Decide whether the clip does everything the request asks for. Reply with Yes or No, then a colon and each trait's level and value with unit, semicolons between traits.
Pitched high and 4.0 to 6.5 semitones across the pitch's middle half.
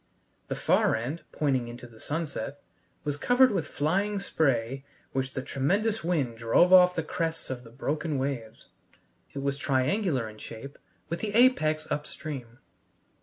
No: medium, 145 Hz; average, 5.0 semitones